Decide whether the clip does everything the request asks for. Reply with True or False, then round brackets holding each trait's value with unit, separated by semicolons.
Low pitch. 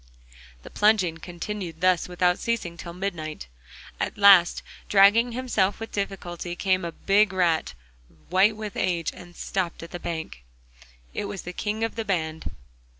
False (185 Hz)